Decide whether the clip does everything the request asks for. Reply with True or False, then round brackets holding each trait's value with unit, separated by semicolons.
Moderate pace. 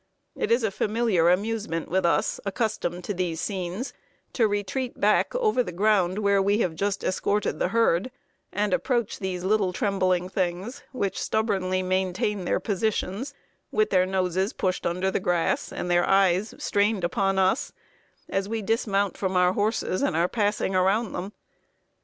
True (160 wpm)